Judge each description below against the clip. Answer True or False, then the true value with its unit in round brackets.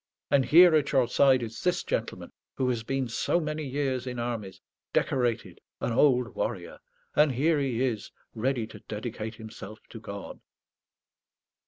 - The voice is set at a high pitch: False (125 Hz)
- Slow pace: False (155 wpm)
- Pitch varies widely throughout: False (3.5 semitones)